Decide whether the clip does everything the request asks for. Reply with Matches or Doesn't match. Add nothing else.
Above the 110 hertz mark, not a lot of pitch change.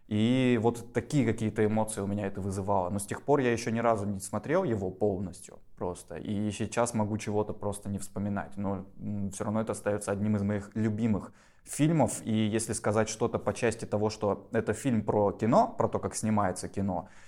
Doesn't match